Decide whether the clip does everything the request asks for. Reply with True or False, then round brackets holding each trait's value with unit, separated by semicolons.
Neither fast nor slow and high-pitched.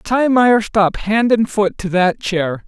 True (155 wpm; 205 Hz)